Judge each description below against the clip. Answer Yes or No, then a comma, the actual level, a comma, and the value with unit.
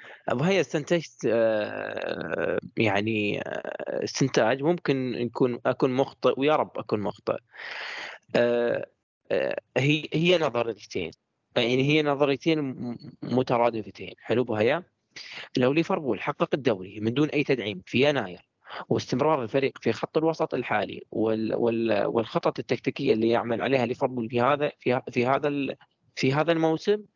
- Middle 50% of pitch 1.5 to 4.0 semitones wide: No, average, 4.6 semitones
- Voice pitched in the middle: No, low, 130 Hz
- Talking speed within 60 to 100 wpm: No, average, 120 wpm